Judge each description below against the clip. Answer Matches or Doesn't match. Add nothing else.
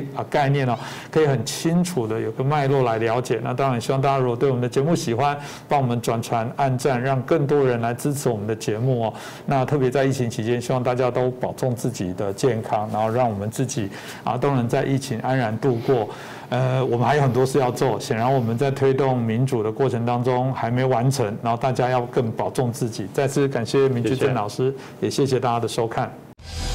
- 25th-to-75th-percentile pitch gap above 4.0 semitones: Doesn't match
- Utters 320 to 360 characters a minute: Matches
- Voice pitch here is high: Doesn't match